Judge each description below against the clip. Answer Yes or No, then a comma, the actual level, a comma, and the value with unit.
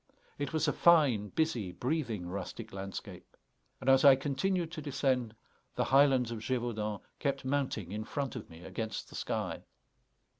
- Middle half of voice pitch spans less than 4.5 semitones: No, average, 5.0 semitones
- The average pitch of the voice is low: Yes, low, 130 Hz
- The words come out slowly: No, average, 155 wpm